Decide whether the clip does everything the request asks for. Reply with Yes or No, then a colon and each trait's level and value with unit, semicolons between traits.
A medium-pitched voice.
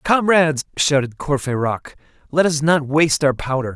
Yes: medium, 145 Hz